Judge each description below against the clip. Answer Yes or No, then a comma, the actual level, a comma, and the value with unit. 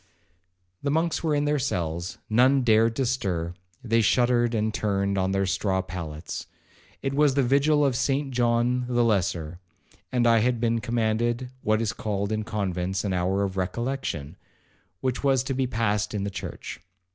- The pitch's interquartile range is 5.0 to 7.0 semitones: No, average, 4.6 semitones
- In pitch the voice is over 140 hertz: No, low, 115 Hz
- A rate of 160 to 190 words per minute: Yes, average, 170 wpm